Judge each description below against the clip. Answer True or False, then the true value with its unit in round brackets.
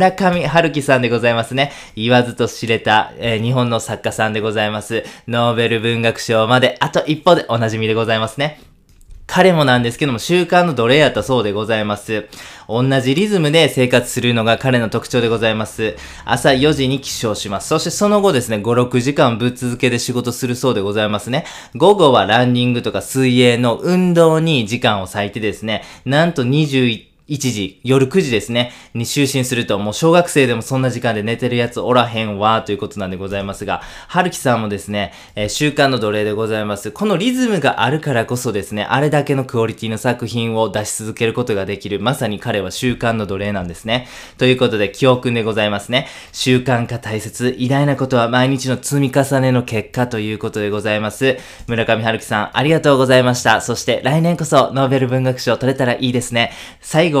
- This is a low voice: True (120 Hz)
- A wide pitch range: False (3.4 semitones)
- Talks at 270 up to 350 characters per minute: False (410 characters per minute)